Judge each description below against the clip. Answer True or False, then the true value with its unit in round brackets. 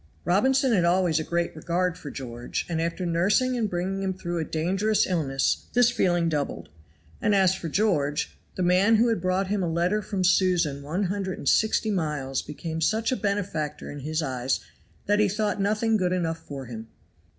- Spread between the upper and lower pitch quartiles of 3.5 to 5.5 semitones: True (4.3 semitones)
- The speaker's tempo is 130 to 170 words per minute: False (190 wpm)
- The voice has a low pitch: False (180 Hz)